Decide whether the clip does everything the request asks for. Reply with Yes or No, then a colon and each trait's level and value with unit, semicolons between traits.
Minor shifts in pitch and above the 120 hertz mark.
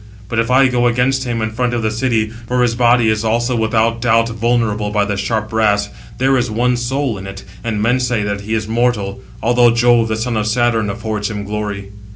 No: narrow, 2.2 semitones; low, 115 Hz